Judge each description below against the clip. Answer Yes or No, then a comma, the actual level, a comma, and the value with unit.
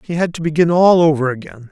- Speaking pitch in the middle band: Yes, medium, 160 Hz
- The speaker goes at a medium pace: No, fast, 245 wpm